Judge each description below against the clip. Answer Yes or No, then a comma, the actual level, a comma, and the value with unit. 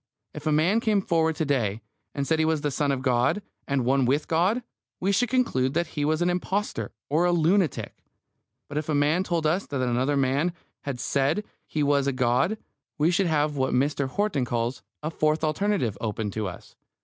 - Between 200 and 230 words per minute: Yes, fast, 205 wpm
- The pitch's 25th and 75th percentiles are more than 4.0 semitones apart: Yes, average, 4.6 semitones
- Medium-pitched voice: Yes, medium, 150 Hz